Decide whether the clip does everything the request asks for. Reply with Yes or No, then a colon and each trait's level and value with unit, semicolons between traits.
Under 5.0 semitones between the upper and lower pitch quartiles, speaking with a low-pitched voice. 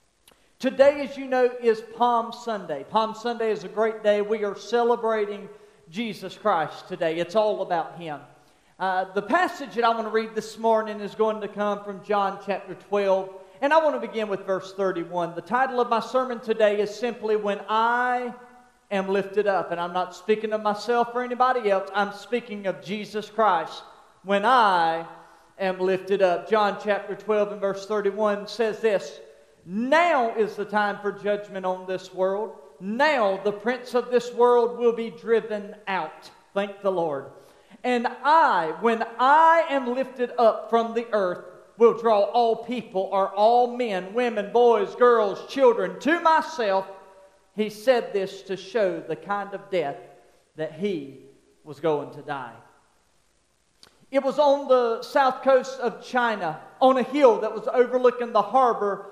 No: average, 3.7 semitones; high, 215 Hz